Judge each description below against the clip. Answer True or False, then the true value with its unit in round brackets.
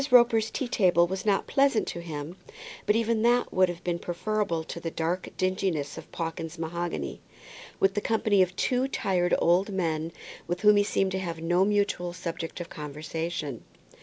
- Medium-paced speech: True (175 wpm)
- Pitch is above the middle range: False (180 Hz)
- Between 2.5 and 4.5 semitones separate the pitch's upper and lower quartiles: True (3.8 semitones)